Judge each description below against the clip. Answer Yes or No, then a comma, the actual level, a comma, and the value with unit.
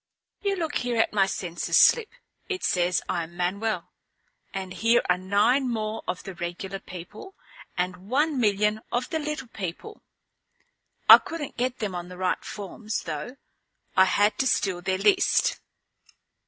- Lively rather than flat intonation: Yes, wide, 5.7 semitones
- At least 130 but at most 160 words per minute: Yes, average, 155 wpm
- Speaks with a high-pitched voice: Yes, high, 210 Hz